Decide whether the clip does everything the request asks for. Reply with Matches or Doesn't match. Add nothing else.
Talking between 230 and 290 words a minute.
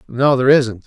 Doesn't match